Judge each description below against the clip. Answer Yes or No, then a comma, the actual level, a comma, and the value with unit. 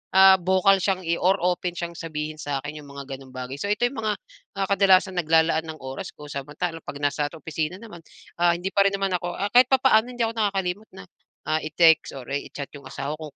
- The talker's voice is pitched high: No, medium, 170 Hz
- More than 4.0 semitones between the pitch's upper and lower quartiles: Yes, average, 4.7 semitones